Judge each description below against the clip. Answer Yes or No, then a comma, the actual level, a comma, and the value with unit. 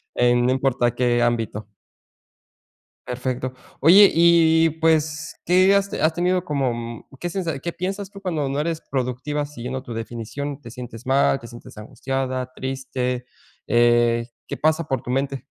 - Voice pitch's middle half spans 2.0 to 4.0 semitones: No, average, 4.8 semitones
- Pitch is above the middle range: No, low, 135 Hz